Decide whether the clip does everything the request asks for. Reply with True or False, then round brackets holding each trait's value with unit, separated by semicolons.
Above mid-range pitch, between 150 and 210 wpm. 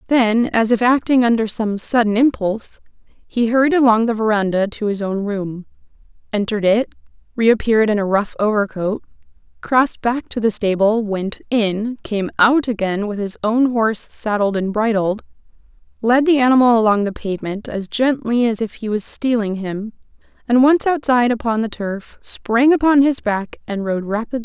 True (225 Hz; 170 wpm)